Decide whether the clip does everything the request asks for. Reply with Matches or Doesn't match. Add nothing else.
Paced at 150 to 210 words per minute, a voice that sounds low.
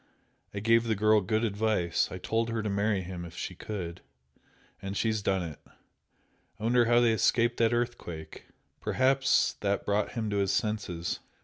Matches